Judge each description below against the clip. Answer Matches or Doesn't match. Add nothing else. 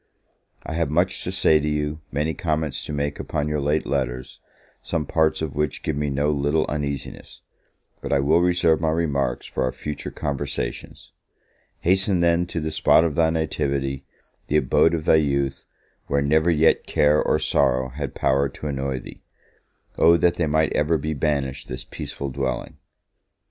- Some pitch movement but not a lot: Doesn't match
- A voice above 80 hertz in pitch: Doesn't match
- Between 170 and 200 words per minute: Matches